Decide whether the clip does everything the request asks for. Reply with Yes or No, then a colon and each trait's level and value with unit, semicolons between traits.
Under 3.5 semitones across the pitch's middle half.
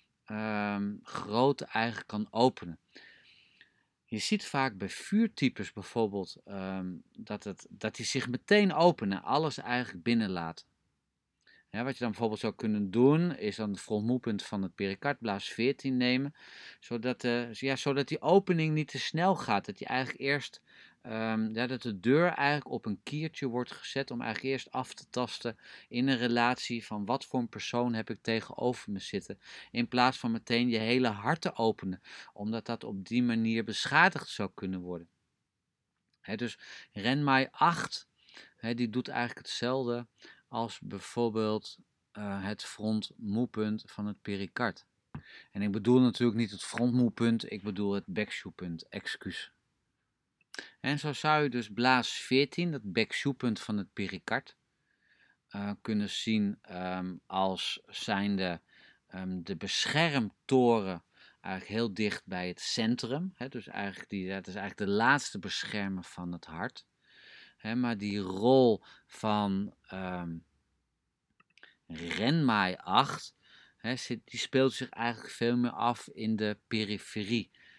No: average, 3.9 semitones